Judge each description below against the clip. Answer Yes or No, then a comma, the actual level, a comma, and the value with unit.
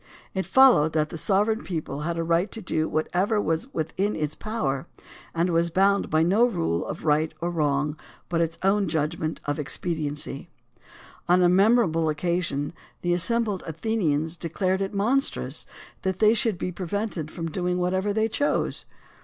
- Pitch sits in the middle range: Yes, medium, 175 Hz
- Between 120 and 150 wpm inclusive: No, average, 165 wpm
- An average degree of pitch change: Yes, average, 4.0 semitones